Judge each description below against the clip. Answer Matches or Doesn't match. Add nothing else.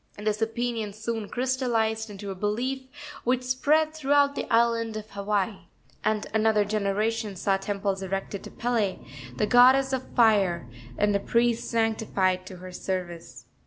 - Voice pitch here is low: Doesn't match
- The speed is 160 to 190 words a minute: Doesn't match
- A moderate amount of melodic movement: Matches